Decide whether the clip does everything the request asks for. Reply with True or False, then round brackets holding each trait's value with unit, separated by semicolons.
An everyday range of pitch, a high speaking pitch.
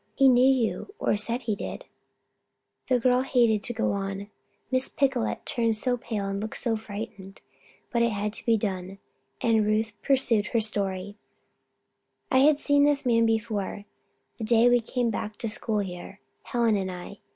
True (3.1 semitones; 225 Hz)